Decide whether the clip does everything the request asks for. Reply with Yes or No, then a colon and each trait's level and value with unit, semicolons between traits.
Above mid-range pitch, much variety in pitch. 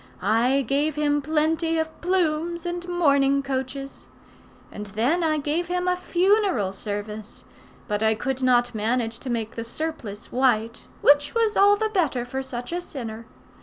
Yes: very high, 275 Hz; wide, 6.1 semitones